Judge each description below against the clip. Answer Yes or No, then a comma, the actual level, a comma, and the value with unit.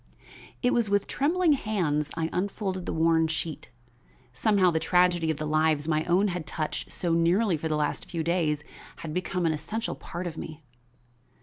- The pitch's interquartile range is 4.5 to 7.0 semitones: No, average, 3.3 semitones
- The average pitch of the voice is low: No, medium, 165 Hz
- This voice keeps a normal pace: Yes, average, 180 wpm